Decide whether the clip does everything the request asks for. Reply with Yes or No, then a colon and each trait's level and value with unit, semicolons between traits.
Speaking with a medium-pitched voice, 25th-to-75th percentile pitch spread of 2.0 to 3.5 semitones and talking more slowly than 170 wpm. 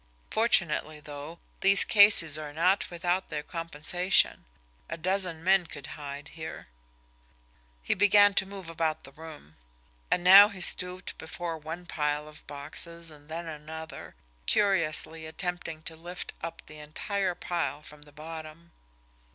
Yes: medium, 165 Hz; average, 3.0 semitones; average, 140 wpm